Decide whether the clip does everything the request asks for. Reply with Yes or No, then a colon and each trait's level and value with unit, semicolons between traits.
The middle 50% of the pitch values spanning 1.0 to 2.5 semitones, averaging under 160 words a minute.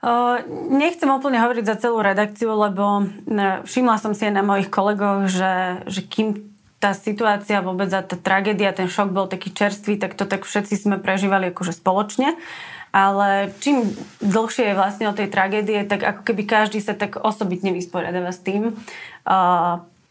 No: narrow, 1.9 semitones; fast, 165 wpm